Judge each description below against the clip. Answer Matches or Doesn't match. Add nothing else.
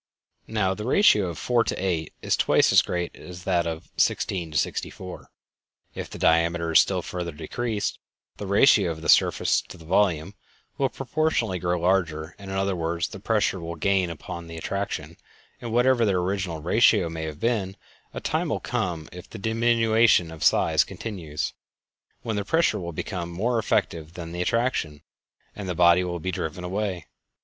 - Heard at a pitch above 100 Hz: Doesn't match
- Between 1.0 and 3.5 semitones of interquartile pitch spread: Doesn't match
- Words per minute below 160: Doesn't match